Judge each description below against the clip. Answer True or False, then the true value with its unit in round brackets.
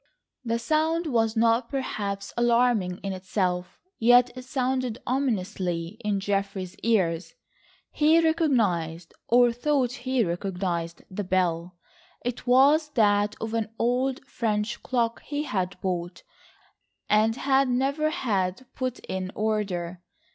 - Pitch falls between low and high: False (225 Hz)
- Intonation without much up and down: False (5.3 semitones)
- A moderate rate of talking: False (120 wpm)